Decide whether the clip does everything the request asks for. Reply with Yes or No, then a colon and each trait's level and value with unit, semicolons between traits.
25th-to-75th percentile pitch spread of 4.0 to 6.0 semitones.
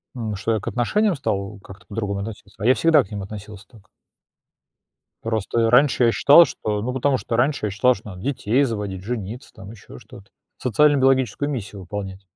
Yes: average, 4.4 semitones